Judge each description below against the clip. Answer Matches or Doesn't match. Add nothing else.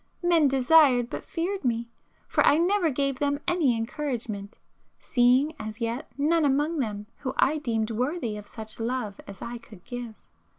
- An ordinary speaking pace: Matches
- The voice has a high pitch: Matches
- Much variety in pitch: Doesn't match